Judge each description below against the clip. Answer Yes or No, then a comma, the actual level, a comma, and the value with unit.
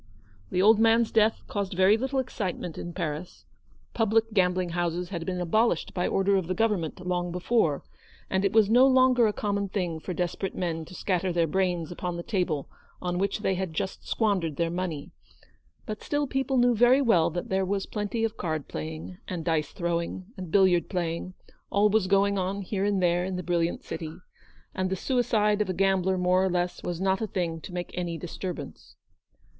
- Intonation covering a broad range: No, average, 3.1 semitones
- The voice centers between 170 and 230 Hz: Yes, medium, 185 Hz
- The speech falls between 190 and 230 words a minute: Yes, average, 195 wpm